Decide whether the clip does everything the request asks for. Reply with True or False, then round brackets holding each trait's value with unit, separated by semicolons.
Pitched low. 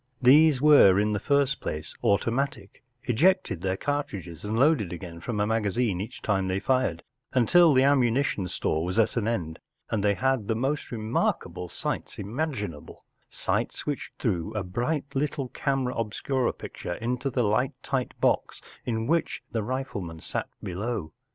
True (115 Hz)